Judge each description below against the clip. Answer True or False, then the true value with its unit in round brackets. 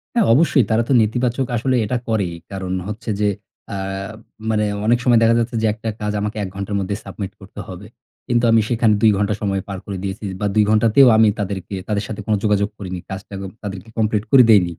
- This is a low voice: True (105 Hz)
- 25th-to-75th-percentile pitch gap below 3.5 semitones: True (2.5 semitones)